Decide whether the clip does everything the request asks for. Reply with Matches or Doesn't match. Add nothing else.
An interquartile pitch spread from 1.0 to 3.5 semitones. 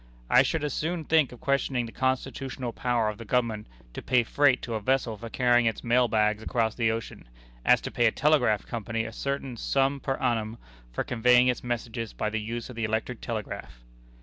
Matches